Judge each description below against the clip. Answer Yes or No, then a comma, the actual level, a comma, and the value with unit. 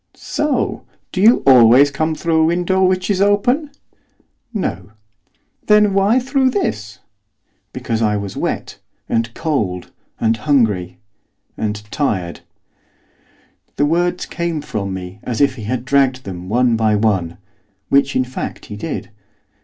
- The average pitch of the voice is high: No, low, 130 Hz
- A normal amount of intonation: No, wide, 8.7 semitones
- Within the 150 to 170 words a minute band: No, average, 140 wpm